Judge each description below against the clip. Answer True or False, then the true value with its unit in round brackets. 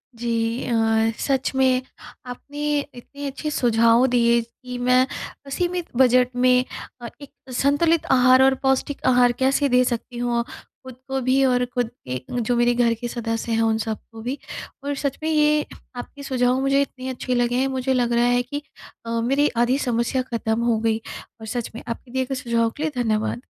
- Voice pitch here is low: False (250 Hz)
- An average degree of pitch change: False (2.2 semitones)